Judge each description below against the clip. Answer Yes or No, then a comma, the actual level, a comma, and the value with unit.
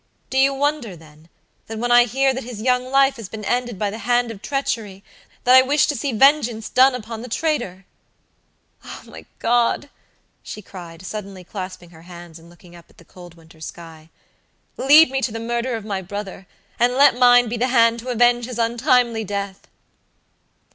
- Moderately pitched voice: No, high, 230 Hz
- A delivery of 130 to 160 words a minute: No, average, 190 wpm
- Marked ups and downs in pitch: No, average, 4.7 semitones